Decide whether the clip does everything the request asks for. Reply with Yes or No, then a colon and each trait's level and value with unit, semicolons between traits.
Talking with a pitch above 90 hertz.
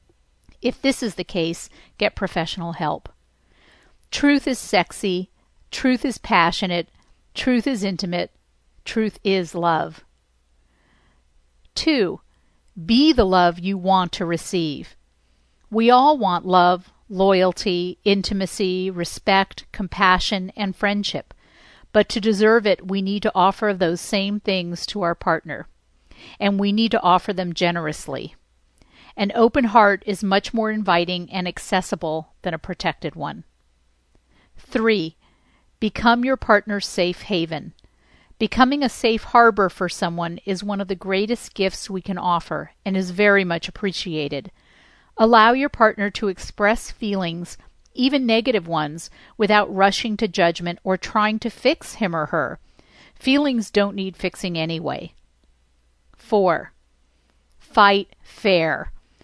Yes: high, 190 Hz